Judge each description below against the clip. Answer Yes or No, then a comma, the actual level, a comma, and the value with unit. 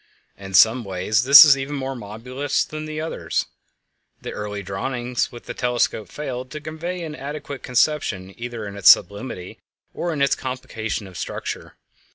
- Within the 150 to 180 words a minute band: Yes, average, 165 wpm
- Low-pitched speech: Yes, low, 125 Hz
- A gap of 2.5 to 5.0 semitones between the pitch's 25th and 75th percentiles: No, wide, 5.6 semitones